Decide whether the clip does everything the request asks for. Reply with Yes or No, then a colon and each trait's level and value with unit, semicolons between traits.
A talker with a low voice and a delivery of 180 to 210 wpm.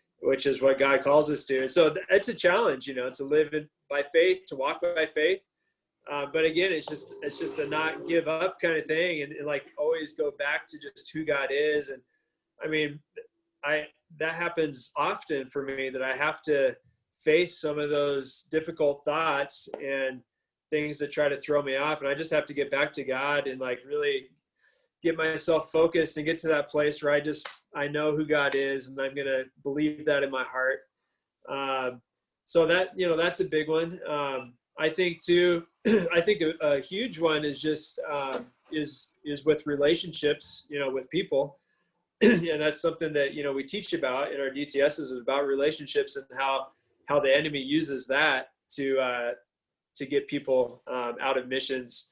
No: medium, 150 Hz; average, 200 wpm